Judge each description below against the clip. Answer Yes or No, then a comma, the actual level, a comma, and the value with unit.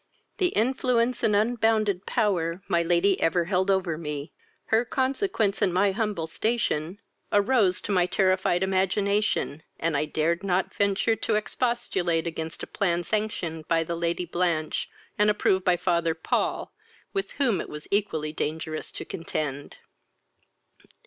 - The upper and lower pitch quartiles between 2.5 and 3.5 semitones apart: No, average, 4.2 semitones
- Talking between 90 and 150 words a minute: Yes, average, 140 wpm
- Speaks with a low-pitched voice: No, medium, 185 Hz